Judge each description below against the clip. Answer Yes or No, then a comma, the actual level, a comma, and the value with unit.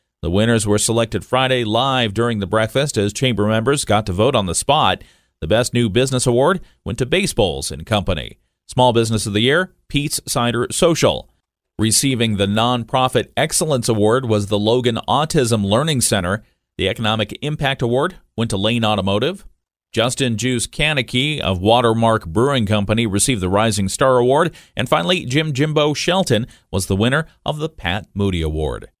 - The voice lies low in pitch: Yes, low, 115 Hz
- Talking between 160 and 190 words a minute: Yes, average, 165 wpm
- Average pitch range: Yes, average, 3.7 semitones